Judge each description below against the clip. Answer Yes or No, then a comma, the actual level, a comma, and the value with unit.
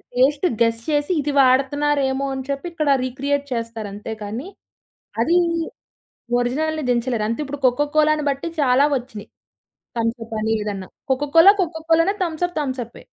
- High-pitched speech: Yes, very high, 270 Hz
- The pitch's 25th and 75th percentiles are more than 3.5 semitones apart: Yes, average, 4.2 semitones